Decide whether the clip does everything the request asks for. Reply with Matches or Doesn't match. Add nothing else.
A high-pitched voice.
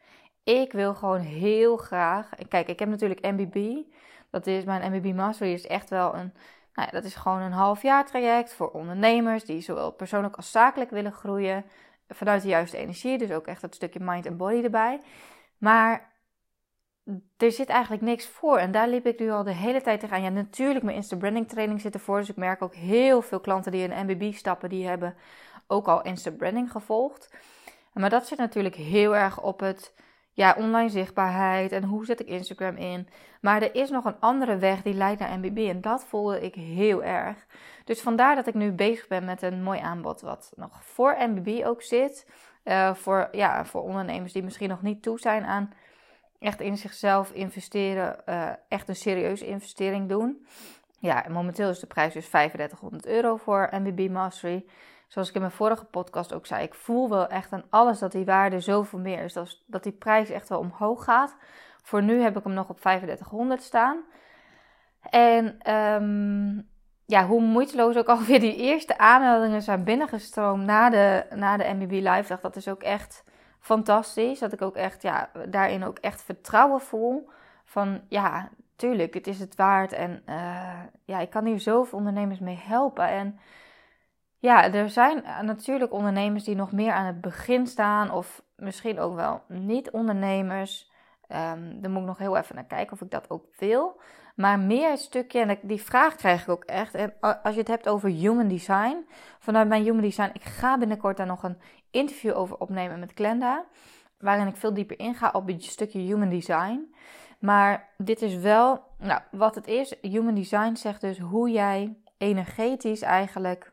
Matches